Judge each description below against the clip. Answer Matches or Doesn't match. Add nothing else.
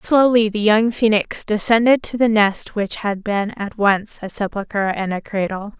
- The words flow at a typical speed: Matches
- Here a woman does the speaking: Matches